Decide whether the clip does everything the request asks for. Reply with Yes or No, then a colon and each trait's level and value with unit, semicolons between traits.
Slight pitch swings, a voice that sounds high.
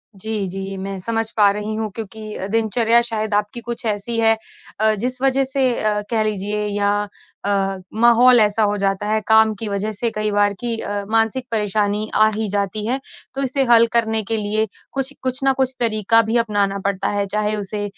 Yes: narrow, 2.0 semitones; high, 215 Hz